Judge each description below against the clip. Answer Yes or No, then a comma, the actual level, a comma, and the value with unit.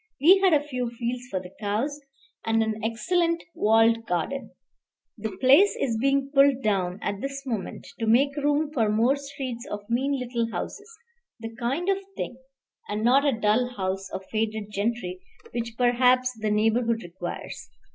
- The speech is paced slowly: No, average, 165 wpm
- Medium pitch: No, high, 235 Hz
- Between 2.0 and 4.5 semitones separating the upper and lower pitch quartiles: Yes, average, 4.1 semitones